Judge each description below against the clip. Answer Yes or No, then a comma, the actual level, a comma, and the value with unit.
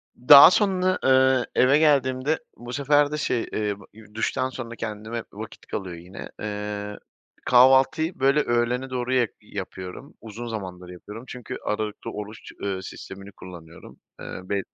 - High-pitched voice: No, low, 115 Hz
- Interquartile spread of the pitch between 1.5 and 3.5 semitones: No, average, 4.3 semitones